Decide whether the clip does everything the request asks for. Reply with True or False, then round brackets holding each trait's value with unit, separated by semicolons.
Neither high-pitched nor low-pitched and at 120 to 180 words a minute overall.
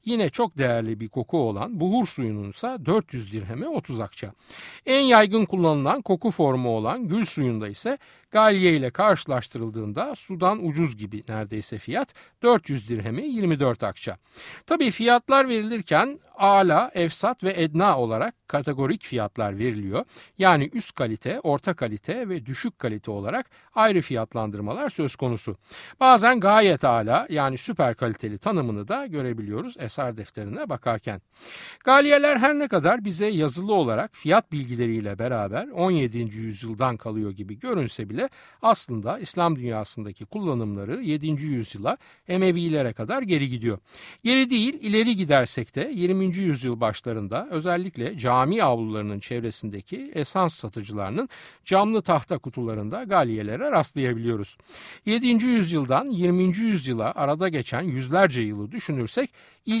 True (145 Hz; 125 wpm)